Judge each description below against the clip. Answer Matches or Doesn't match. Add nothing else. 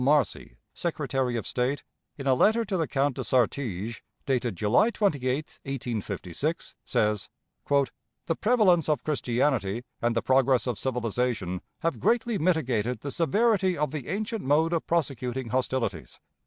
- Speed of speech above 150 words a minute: Doesn't match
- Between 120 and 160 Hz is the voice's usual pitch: Matches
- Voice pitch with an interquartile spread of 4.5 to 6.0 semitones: Matches